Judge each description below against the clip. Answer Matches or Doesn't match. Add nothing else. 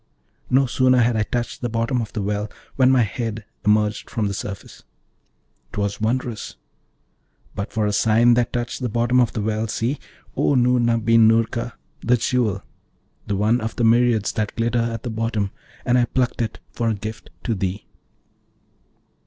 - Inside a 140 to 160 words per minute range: Doesn't match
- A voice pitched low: Matches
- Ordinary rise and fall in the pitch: Doesn't match